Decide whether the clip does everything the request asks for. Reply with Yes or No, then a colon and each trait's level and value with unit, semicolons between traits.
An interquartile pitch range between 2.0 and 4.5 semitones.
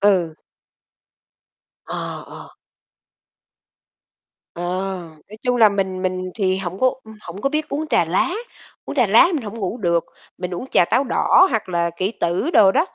No: average, 4.9 semitones